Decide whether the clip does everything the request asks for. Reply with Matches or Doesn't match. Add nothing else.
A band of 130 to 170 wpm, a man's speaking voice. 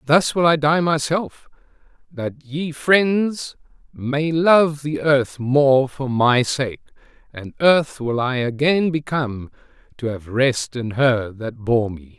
Matches